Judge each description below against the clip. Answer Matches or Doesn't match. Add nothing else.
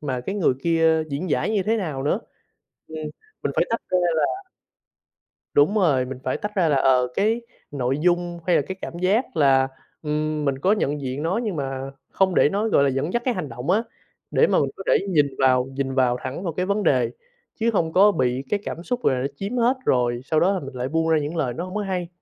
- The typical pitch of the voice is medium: Matches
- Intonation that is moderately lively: Doesn't match